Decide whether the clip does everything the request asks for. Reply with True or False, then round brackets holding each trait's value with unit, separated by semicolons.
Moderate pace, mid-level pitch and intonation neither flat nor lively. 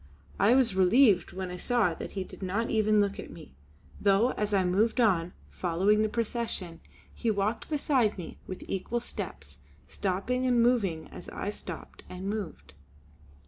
False (165 wpm; 205 Hz; 4.0 semitones)